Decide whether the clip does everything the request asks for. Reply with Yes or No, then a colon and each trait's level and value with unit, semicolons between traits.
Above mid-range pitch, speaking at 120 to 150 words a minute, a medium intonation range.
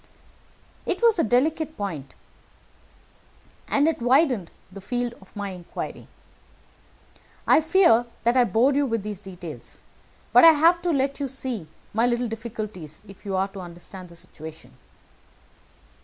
No: high, 230 Hz; average, 145 wpm; wide, 6.5 semitones